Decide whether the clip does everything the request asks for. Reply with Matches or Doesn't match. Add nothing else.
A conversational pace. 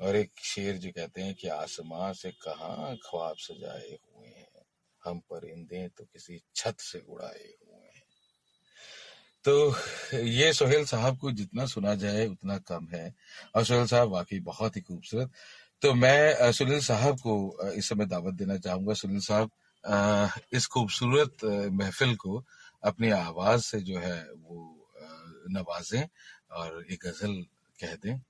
Matches